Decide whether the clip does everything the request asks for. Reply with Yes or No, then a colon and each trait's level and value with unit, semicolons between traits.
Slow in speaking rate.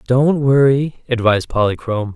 Yes: slow, 110 wpm